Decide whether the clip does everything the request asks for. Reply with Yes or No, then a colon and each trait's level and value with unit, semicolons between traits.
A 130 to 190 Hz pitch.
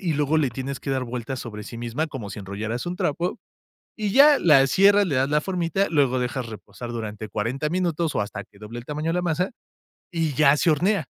Yes: medium, 140 Hz